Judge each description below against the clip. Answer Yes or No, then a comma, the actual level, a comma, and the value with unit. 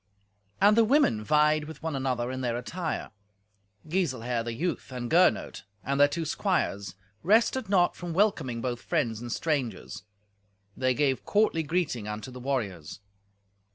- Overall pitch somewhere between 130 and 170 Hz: Yes, medium, 140 Hz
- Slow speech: No, average, 150 wpm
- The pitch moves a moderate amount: No, wide, 6.1 semitones